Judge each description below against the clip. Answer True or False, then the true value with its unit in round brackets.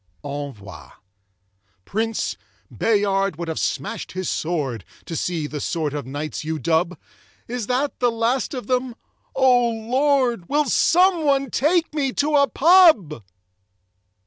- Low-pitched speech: False (225 Hz)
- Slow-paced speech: True (130 wpm)